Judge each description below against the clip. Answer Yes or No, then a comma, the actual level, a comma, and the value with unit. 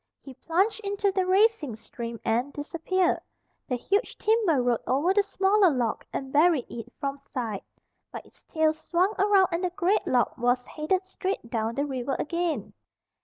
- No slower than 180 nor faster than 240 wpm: No, average, 170 wpm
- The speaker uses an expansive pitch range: Yes, wide, 7.3 semitones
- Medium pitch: No, very high, 315 Hz